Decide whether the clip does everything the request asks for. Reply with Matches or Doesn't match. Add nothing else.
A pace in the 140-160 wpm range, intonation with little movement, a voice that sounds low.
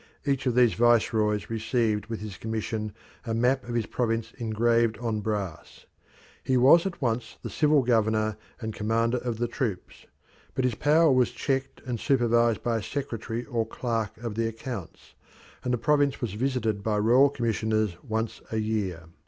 Doesn't match